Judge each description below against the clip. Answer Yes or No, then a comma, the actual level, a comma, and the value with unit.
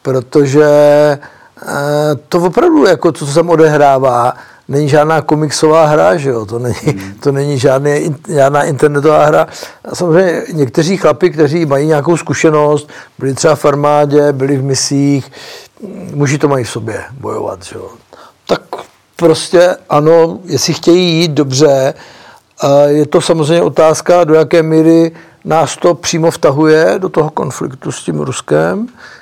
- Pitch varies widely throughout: No, average, 2.7 semitones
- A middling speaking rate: Yes, average, 145 wpm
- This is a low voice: No, medium, 150 Hz